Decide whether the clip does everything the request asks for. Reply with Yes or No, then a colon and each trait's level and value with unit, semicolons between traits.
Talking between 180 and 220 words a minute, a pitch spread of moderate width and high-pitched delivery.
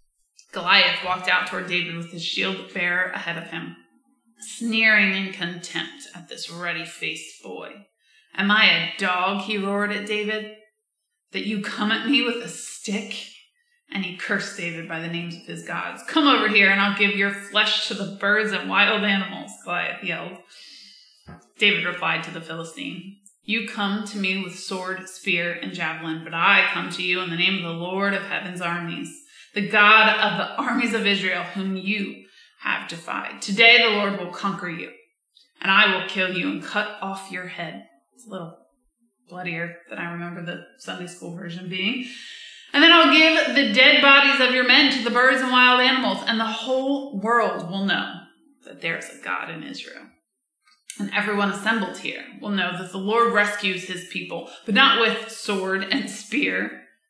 Yes: average, 185 wpm; average, 4.1 semitones; high, 200 Hz